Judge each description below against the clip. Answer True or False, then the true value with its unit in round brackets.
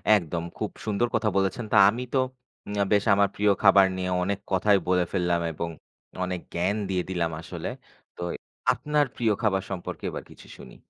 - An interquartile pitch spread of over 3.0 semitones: False (2.7 semitones)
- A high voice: False (95 Hz)